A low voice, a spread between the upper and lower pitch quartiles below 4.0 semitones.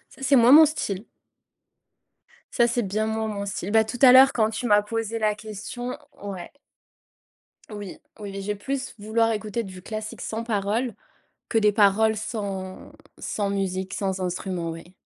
No: high, 215 Hz; narrow, 2.5 semitones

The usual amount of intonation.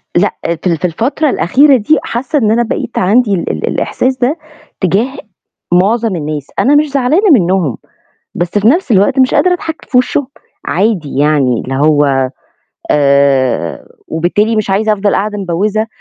No: wide, 7.4 semitones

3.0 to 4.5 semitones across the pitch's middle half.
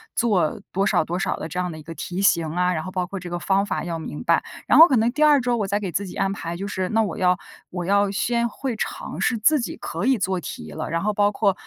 Yes: average, 3.6 semitones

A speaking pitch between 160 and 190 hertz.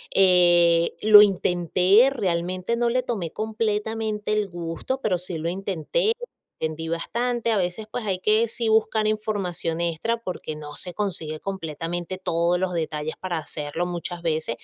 Yes: medium, 185 Hz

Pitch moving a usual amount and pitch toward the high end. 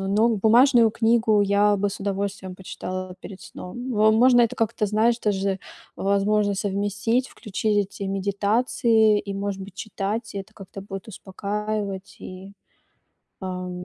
No: narrow, 2.0 semitones; high, 205 Hz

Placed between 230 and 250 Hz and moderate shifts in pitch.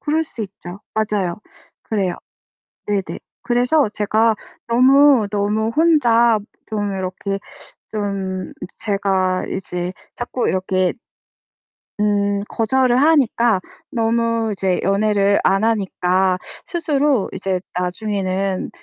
No: high, 205 Hz; average, 3.5 semitones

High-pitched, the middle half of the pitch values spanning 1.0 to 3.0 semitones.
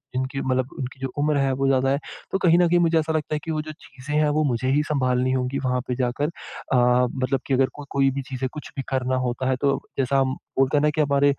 No: low, 135 Hz; narrow, 2.5 semitones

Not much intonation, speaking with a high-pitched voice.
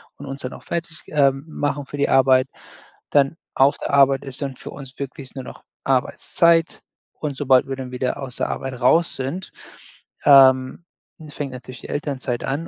No: narrow, 1.8 semitones; low, 135 Hz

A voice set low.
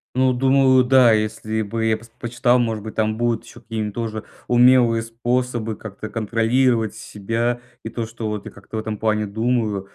Yes: low, 115 Hz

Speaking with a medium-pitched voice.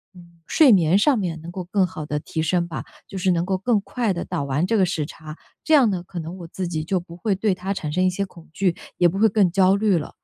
Yes: medium, 180 Hz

